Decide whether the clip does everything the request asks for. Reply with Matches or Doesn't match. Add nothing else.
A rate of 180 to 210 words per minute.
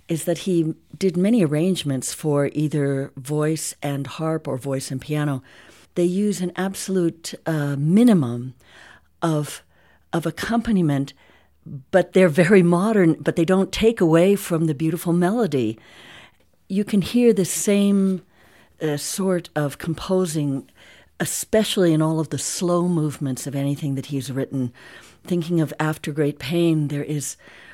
Doesn't match